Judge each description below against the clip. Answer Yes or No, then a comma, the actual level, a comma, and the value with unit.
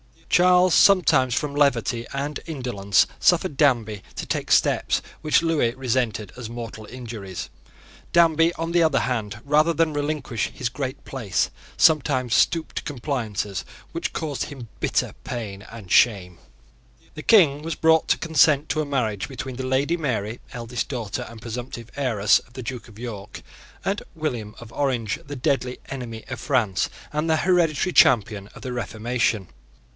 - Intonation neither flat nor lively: Yes, average, 4.9 semitones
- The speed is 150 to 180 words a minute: Yes, average, 155 wpm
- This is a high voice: No, low, 130 Hz